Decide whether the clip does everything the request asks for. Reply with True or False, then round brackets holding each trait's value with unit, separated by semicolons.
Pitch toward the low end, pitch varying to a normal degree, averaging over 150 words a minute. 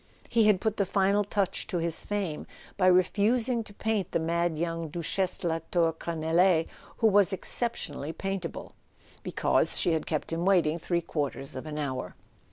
False (175 Hz; 3.6 semitones; 170 wpm)